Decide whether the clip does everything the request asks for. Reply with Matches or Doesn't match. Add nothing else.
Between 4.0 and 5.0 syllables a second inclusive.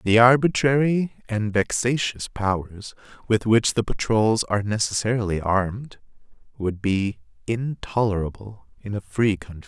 Matches